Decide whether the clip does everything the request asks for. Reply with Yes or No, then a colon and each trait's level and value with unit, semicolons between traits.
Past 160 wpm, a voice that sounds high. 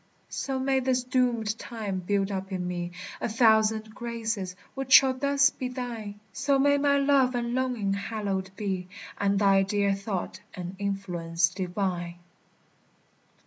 No: average, 145 wpm; high, 215 Hz